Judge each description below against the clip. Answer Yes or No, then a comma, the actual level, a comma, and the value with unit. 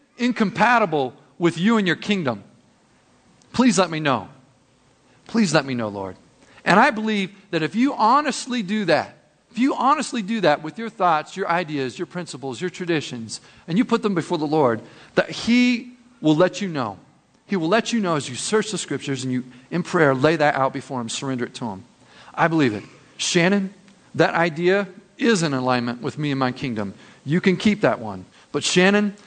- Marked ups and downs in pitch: Yes, wide, 7.9 semitones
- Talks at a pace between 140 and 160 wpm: No, average, 195 wpm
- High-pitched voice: No, medium, 170 Hz